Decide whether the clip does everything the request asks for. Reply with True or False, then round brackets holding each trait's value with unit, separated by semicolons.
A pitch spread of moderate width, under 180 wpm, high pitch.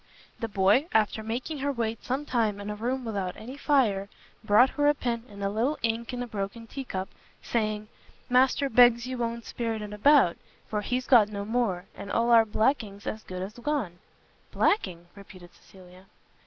False (3.7 semitones; 185 wpm; 225 Hz)